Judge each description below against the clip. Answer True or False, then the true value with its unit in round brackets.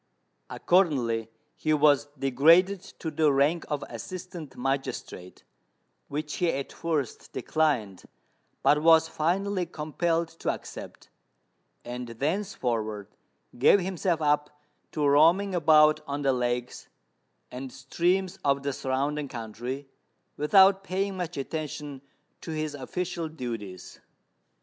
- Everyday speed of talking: False (110 wpm)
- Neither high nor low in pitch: True (150 Hz)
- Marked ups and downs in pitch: False (4.2 semitones)